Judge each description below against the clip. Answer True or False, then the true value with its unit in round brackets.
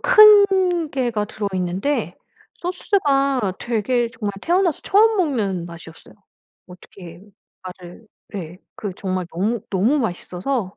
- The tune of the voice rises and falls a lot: True (8.4 semitones)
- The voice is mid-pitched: False (225 Hz)